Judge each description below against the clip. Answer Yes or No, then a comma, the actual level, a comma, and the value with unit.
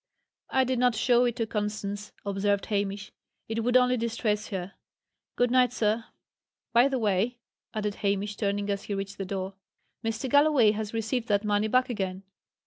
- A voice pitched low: No, high, 215 Hz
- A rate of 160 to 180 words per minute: Yes, average, 170 wpm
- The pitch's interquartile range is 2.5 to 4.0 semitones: Yes, average, 3.2 semitones